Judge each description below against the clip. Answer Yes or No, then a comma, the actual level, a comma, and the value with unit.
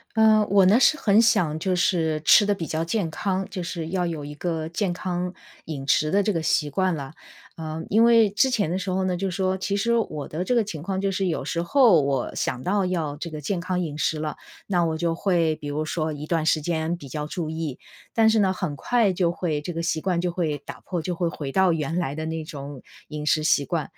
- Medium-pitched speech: Yes, medium, 170 Hz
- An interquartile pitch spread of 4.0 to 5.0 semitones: No, average, 3.5 semitones